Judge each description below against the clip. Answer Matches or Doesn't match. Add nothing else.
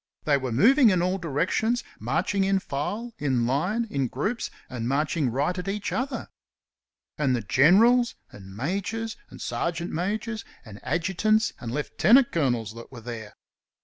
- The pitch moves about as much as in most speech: Doesn't match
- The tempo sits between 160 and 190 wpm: Doesn't match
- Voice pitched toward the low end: Doesn't match